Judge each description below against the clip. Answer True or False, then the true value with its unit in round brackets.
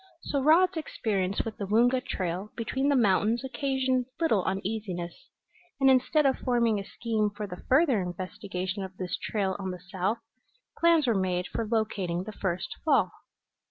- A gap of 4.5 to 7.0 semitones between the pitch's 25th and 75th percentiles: True (5.5 semitones)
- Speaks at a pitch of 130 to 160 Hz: False (215 Hz)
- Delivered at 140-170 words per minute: True (160 wpm)